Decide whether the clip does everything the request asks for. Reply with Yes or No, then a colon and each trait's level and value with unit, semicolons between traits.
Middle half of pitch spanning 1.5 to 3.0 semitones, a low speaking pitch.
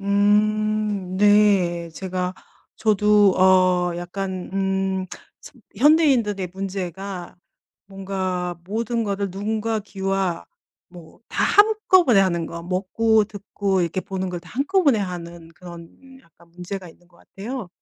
No: average, 2.7 semitones; high, 195 Hz